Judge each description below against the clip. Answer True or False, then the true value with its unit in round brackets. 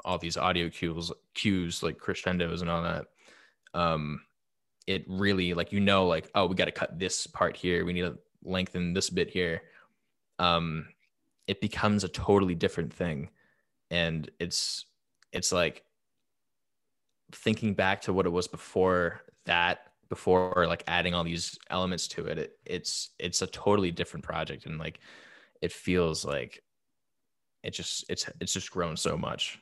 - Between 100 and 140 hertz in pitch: False (90 Hz)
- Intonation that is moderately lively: False (1.7 semitones)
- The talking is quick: False (160 wpm)